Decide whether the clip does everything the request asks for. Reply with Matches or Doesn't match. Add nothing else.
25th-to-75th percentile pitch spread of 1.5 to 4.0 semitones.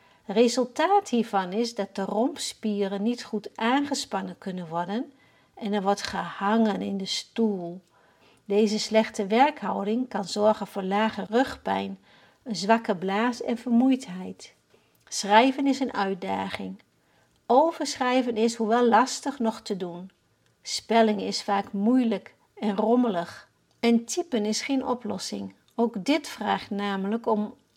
Matches